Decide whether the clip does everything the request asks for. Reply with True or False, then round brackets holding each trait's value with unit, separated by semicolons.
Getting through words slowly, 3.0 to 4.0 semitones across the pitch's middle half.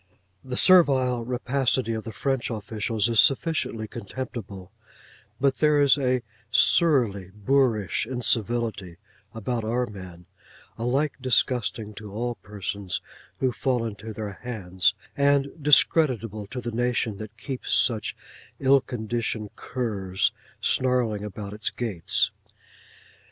True (115 wpm; 3.6 semitones)